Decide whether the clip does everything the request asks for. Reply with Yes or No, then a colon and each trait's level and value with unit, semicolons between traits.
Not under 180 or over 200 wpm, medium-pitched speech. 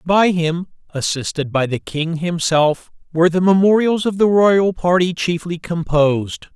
No: average, 145 wpm; medium, 170 Hz